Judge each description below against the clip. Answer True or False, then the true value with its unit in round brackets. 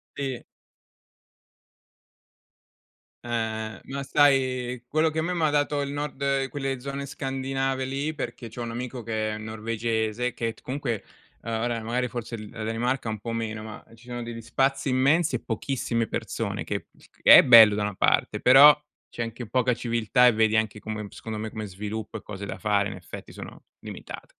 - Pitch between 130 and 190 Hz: False (120 Hz)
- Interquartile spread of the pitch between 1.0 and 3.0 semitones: False (3.4 semitones)